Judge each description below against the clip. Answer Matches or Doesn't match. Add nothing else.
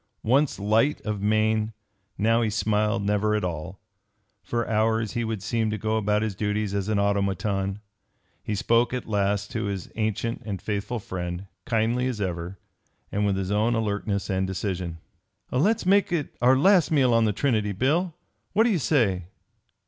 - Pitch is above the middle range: Doesn't match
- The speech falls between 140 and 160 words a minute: Doesn't match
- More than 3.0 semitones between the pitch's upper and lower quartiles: Doesn't match